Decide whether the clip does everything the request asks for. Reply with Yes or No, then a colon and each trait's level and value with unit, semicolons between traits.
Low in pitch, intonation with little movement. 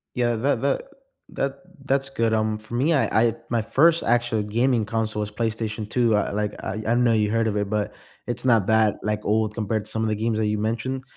Yes: low, 110 Hz; narrow, 2.1 semitones